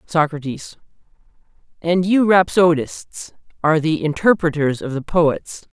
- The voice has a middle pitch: Yes, medium, 165 Hz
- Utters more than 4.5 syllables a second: No, 4.2 syllables/s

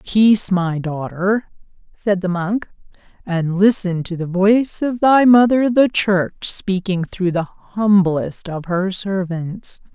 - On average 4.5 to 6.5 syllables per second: No, 3.6 syllables/s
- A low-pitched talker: No, high, 190 Hz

